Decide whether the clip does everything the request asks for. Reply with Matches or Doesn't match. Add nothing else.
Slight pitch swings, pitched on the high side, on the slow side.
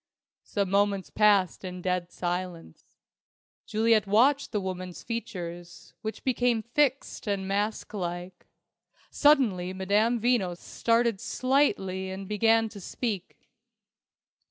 Doesn't match